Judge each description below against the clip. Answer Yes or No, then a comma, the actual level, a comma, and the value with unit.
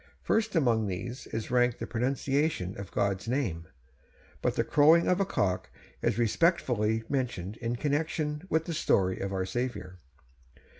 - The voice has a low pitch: Yes, low, 120 Hz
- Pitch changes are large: Yes, wide, 7.0 semitones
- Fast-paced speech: No, average, 150 wpm